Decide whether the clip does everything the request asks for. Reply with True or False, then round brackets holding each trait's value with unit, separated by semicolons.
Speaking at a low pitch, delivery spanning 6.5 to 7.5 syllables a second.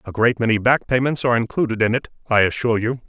True (115 Hz; 7.0 syllables/s)